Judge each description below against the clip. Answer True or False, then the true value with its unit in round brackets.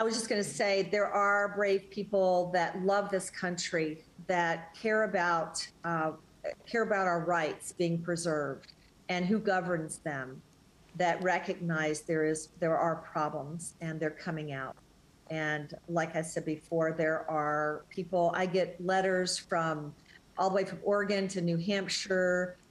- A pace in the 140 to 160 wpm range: True (155 wpm)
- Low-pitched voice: False (175 Hz)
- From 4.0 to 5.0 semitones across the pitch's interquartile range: False (3.0 semitones)